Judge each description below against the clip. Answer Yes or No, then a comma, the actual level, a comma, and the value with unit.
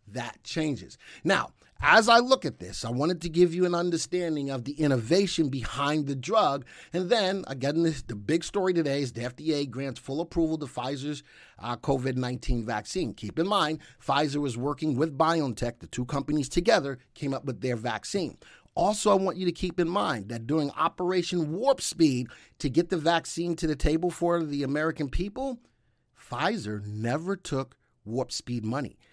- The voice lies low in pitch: No, medium, 150 Hz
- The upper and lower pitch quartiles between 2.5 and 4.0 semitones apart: No, average, 5.0 semitones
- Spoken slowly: No, average, 180 wpm